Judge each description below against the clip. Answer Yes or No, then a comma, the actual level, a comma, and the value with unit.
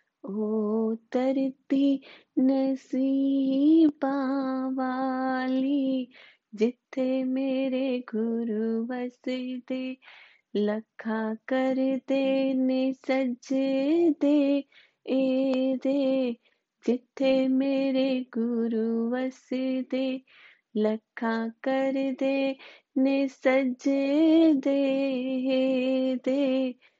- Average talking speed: No, slow, 50 wpm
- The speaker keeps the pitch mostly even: Yes, narrow, 1.1 semitones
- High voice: Yes, very high, 260 Hz